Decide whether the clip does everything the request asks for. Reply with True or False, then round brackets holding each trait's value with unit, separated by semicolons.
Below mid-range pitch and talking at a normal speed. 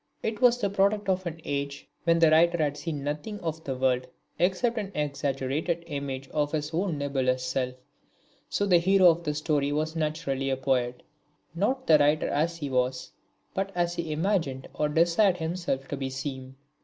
False (155 Hz; 180 wpm)